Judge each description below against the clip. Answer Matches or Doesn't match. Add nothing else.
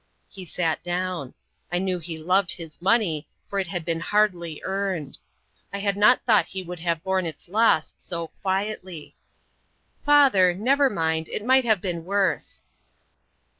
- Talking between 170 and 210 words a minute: Doesn't match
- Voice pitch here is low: Doesn't match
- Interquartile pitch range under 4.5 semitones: Matches